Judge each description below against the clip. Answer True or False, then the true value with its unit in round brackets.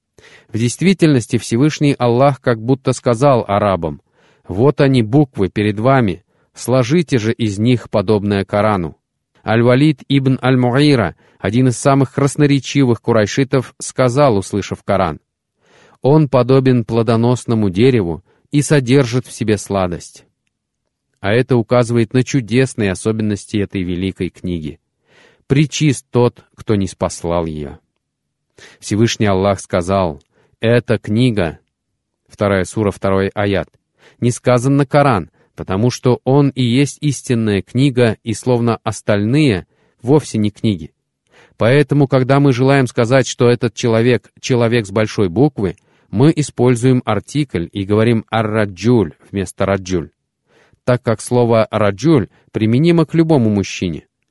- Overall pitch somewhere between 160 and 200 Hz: False (120 Hz)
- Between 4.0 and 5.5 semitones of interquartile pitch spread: True (4.7 semitones)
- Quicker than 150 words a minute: False (120 wpm)